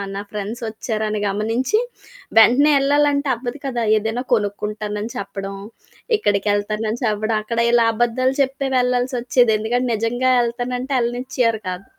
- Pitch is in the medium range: No, high, 235 Hz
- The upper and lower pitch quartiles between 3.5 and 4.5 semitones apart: No, average, 2.9 semitones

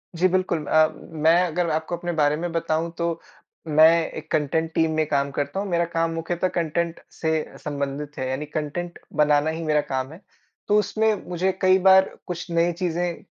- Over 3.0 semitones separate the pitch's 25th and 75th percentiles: No, narrow, 2.5 semitones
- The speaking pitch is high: No, medium, 165 Hz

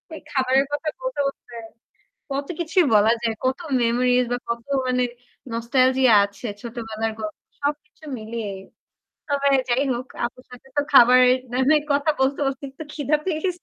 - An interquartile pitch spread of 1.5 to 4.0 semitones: Yes, average, 3.3 semitones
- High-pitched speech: Yes, very high, 255 Hz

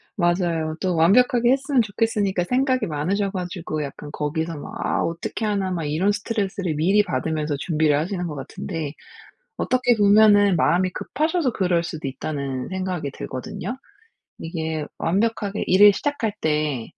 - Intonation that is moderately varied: Yes, average, 4.9 semitones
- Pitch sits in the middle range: Yes, medium, 180 Hz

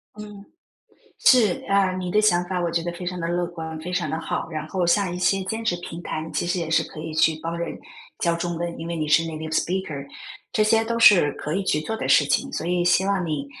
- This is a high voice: No, medium, 175 Hz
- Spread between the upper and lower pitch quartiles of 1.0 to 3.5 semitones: Yes, average, 2.7 semitones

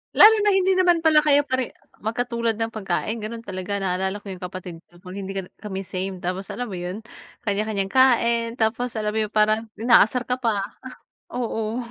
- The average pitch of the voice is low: No, high, 220 Hz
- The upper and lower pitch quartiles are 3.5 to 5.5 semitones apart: Yes, average, 4.1 semitones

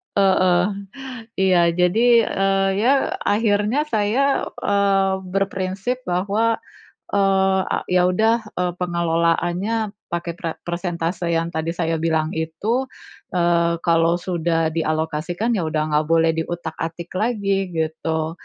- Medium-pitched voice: Yes, medium, 180 Hz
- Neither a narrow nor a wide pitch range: Yes, average, 3.3 semitones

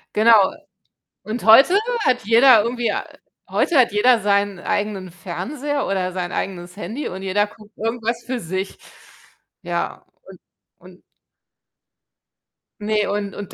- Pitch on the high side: Yes, high, 210 Hz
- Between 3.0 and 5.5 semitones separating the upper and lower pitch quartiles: Yes, average, 3.7 semitones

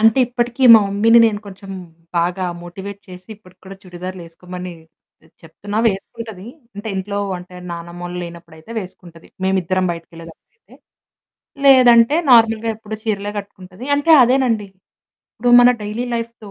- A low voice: No, high, 200 Hz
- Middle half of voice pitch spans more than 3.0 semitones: Yes, average, 4.1 semitones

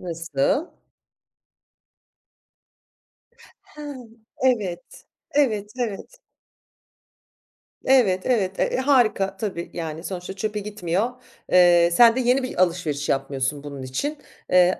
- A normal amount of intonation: No, wide, 6.0 semitones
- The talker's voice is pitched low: No, high, 190 Hz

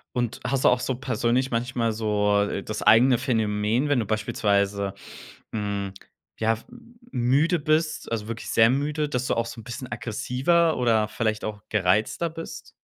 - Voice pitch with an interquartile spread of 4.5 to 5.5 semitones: No, average, 3.5 semitones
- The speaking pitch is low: Yes, low, 115 Hz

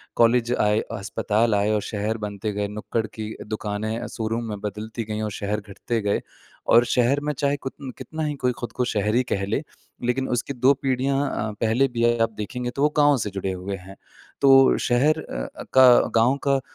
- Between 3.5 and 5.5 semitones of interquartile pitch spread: Yes, average, 3.8 semitones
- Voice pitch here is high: No, low, 115 Hz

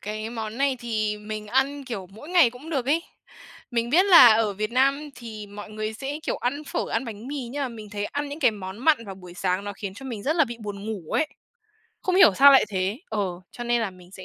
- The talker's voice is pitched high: Yes, high, 230 Hz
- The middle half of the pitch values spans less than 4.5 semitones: No, average, 4.8 semitones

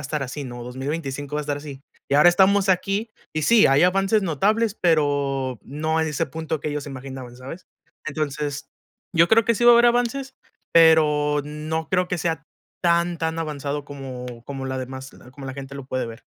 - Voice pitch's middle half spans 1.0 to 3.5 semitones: No, average, 4.1 semitones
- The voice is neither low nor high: Yes, medium, 150 Hz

